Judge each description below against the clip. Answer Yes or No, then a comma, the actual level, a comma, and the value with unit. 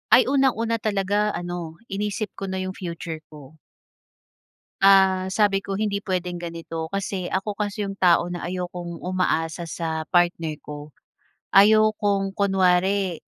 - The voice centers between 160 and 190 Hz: Yes, medium, 185 Hz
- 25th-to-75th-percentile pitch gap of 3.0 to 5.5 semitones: No, narrow, 2.6 semitones